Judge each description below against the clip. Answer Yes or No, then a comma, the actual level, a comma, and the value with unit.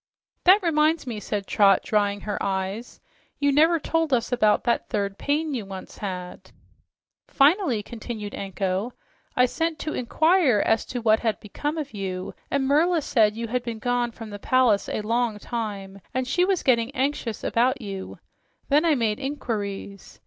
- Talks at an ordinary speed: Yes, average, 170 wpm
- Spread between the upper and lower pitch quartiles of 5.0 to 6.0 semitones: Yes, wide, 5.6 semitones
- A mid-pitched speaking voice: No, high, 235 Hz